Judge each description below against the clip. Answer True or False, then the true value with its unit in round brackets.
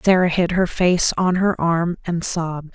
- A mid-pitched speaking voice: True (175 Hz)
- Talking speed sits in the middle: True (195 wpm)